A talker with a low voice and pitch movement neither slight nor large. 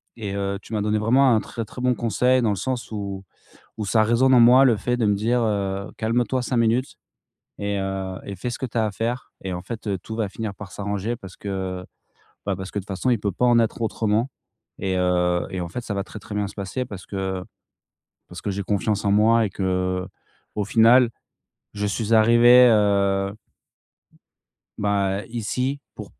Yes: low, 105 Hz; average, 3.1 semitones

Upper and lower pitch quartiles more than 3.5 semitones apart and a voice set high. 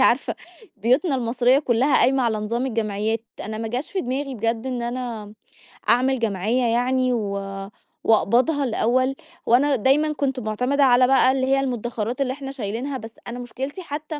No: average, 2.9 semitones; very high, 250 Hz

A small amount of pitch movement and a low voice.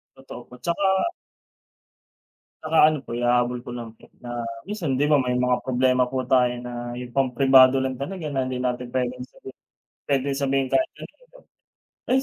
Yes: narrow, 2.1 semitones; low, 130 Hz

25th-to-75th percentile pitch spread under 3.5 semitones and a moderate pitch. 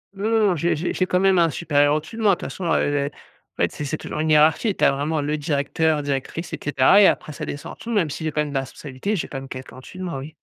No: average, 4.0 semitones; medium, 155 Hz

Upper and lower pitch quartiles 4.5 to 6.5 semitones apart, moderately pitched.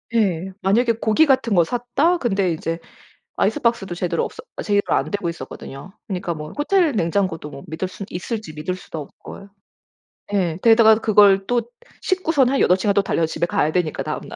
No: wide, 5.5 semitones; high, 195 Hz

